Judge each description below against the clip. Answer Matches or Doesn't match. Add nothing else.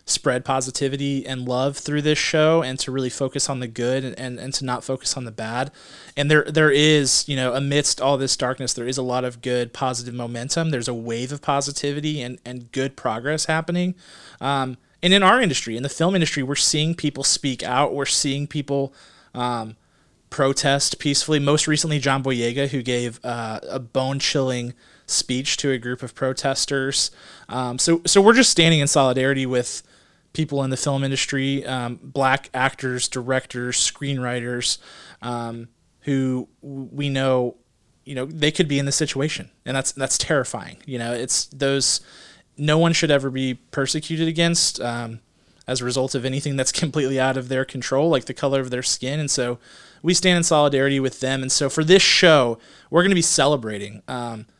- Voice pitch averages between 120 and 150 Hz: Matches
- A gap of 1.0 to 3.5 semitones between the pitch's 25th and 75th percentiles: Matches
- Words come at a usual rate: Matches